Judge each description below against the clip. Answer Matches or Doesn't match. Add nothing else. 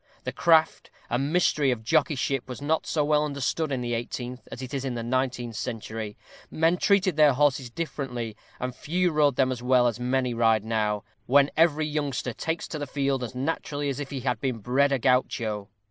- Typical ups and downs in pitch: Matches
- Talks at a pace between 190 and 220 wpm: Matches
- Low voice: Matches